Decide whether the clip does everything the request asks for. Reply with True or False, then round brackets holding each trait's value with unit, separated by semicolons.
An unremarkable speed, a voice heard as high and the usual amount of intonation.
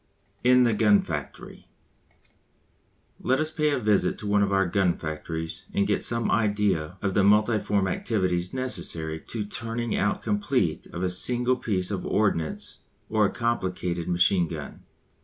False (160 wpm; 100 Hz; 4.5 semitones)